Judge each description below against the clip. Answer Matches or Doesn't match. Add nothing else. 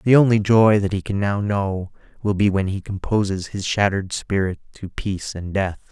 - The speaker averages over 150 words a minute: Matches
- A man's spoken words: Matches